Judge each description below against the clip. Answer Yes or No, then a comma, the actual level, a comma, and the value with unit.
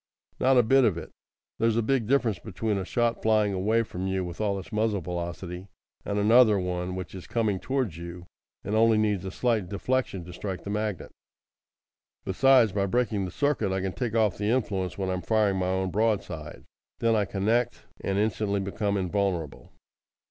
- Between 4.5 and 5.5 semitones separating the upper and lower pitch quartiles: No, average, 3.3 semitones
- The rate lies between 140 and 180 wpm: No, average, 190 wpm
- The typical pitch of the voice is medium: No, low, 100 Hz